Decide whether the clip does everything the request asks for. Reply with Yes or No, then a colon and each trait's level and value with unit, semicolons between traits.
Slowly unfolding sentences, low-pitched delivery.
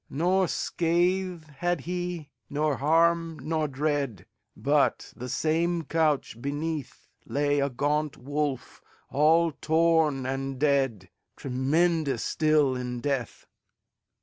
No: slow, 95 wpm; medium, 150 Hz